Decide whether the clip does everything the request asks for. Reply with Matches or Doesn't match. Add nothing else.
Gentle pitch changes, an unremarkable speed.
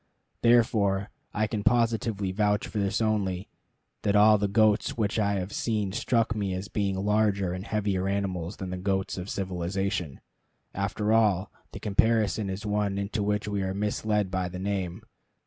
Matches